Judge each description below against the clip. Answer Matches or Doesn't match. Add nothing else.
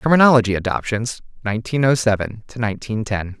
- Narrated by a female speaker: Doesn't match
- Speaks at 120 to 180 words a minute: Matches